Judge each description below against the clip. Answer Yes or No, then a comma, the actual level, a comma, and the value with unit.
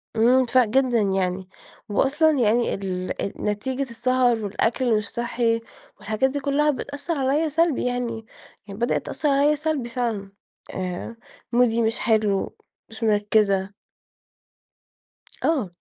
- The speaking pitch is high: Yes, high, 235 Hz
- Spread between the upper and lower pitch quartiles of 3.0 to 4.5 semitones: Yes, average, 4.2 semitones